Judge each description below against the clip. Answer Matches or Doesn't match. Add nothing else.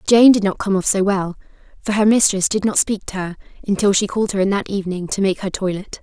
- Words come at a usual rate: Doesn't match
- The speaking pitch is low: Doesn't match